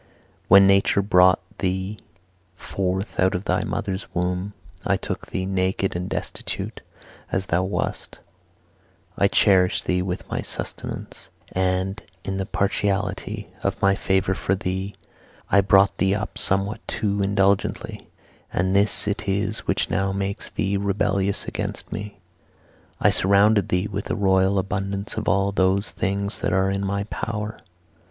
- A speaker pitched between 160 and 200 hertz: No, very low, 95 Hz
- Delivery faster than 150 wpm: No, average, 145 wpm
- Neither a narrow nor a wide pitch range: No, narrow, 1.1 semitones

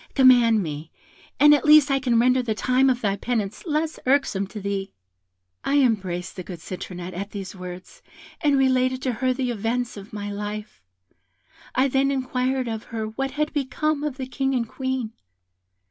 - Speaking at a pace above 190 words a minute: No, average, 175 wpm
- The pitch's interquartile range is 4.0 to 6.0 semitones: Yes, average, 4.8 semitones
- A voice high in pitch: Yes, high, 245 Hz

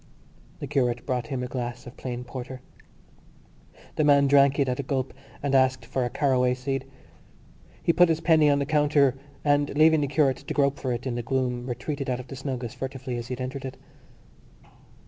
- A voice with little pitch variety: Yes, narrow, 2.1 semitones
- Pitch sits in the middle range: No, low, 130 Hz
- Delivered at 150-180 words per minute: No, fast, 205 wpm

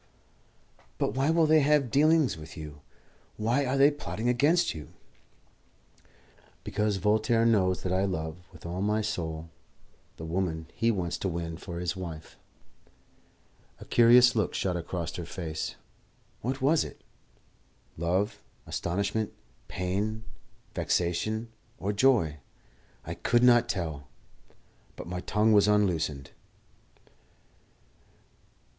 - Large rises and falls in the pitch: Yes, wide, 5.7 semitones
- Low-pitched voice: Yes, low, 100 Hz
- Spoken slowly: Yes, slow, 120 wpm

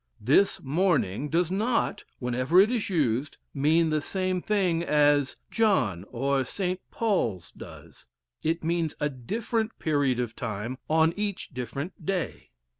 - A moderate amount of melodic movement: No, wide, 6.3 semitones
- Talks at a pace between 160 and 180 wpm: No, slow, 135 wpm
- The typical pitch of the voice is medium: Yes, medium, 160 Hz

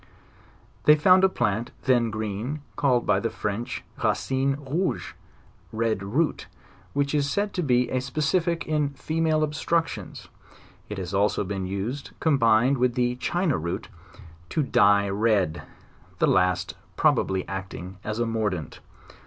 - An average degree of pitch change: No, wide, 6.4 semitones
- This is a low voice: Yes, low, 120 Hz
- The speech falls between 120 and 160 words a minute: Yes, average, 140 wpm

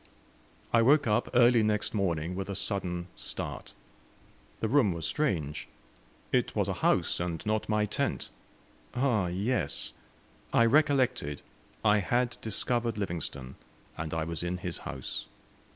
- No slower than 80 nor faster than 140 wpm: Yes, slow, 135 wpm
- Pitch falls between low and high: No, low, 105 Hz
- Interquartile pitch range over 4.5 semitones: Yes, wide, 5.5 semitones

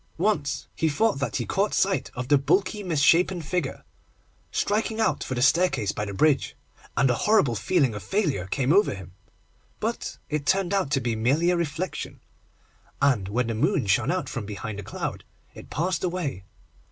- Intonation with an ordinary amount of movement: No, wide, 7.4 semitones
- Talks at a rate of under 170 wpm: No, average, 180 wpm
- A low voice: No, medium, 145 Hz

